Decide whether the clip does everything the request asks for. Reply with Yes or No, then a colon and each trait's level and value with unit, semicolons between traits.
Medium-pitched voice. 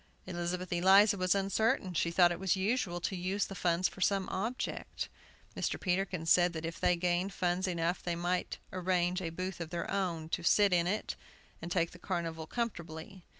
Yes: medium, 180 Hz